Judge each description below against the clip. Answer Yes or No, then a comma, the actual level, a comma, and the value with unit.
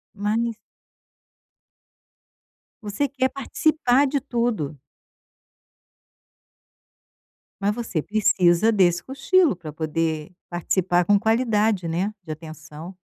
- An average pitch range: No, wide, 5.8 semitones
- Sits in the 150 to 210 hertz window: Yes, high, 200 Hz